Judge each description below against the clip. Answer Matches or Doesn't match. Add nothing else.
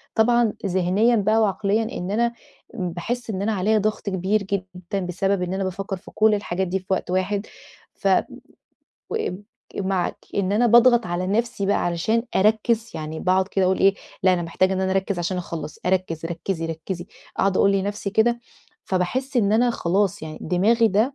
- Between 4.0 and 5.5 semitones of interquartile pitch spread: Doesn't match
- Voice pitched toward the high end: Matches